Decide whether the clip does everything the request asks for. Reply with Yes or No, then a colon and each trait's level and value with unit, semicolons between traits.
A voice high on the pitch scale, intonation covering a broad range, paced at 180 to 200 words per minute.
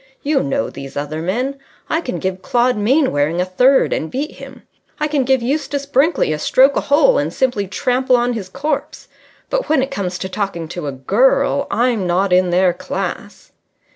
Yes: high, 245 Hz; wide, 7.1 semitones; average, 190 wpm